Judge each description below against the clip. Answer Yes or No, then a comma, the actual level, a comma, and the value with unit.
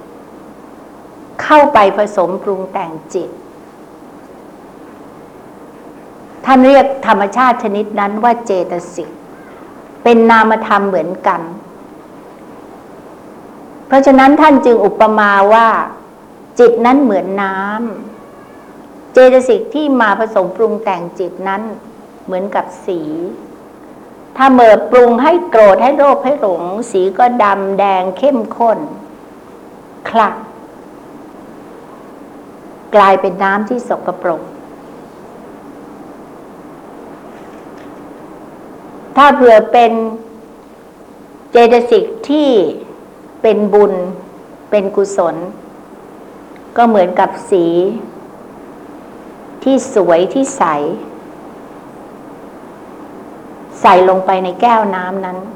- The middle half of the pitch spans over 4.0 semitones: Yes, average, 4.6 semitones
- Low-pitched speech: No, high, 220 Hz